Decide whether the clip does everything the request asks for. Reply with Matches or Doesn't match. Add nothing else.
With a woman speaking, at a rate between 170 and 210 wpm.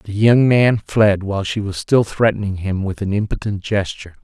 Doesn't match